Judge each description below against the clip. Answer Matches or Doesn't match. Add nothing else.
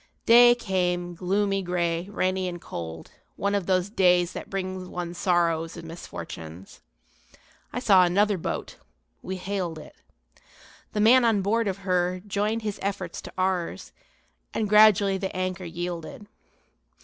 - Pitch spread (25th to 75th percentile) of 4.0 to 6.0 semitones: Doesn't match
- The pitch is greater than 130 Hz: Matches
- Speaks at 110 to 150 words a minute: Matches